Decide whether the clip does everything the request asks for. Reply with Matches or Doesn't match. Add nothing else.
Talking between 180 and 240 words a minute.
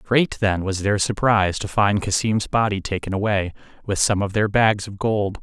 Matches